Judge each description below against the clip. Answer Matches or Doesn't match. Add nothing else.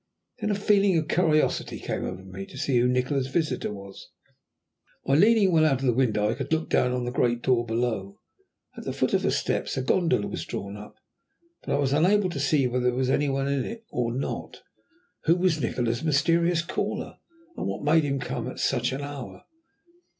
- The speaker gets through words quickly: Matches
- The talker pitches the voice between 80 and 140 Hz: Matches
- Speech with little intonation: Doesn't match